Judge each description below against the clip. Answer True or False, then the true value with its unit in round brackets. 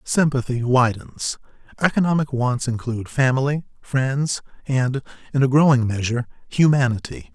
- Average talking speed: False (105 wpm)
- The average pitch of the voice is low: True (130 Hz)